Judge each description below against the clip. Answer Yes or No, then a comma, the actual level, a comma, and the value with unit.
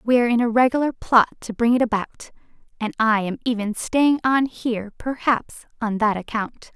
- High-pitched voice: Yes, high, 235 Hz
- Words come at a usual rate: Yes, average, 185 wpm